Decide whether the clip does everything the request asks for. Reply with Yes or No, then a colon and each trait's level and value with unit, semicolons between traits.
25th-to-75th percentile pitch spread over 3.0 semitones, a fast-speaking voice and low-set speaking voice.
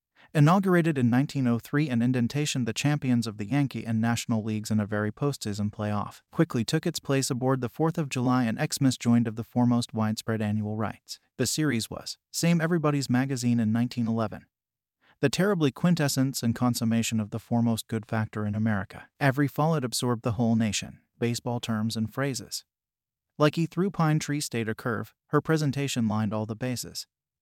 No: average, 4.4 semitones; average, 175 wpm; low, 120 Hz